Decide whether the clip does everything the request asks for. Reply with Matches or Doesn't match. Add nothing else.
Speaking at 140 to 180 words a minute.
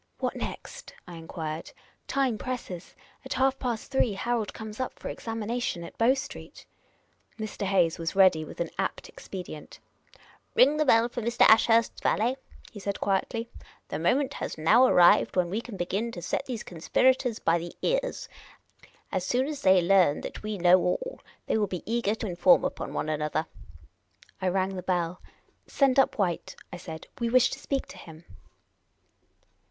Doesn't match